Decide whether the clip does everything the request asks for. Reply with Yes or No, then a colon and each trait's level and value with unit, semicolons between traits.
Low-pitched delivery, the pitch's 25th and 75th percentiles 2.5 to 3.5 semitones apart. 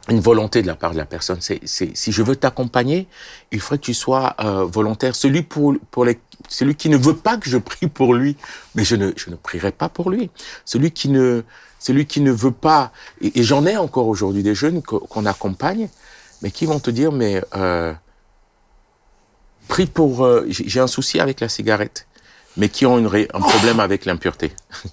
No: low, 125 Hz; wide, 5.4 semitones